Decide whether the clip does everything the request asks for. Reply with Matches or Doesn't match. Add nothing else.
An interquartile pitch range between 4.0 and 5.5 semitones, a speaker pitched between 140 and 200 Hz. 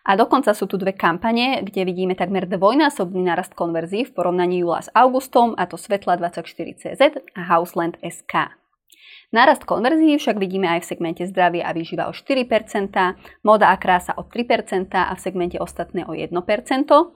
Matches